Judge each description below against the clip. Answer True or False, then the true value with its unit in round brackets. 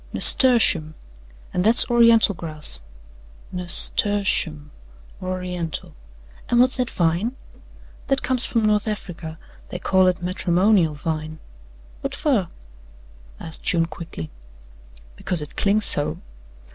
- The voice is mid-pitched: True (180 Hz)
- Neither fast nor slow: False (115 wpm)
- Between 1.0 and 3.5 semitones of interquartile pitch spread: False (4.9 semitones)